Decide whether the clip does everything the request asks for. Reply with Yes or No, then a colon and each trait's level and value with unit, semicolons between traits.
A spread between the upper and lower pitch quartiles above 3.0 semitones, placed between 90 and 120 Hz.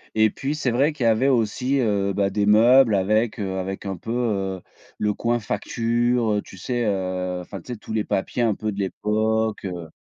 Yes: average, 3.4 semitones; low, 110 Hz